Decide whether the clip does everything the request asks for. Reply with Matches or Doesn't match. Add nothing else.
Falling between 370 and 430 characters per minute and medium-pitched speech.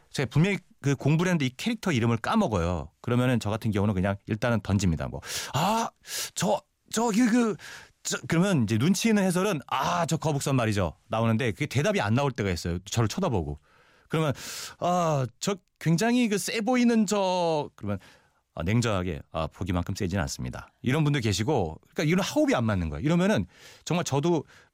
Doesn't match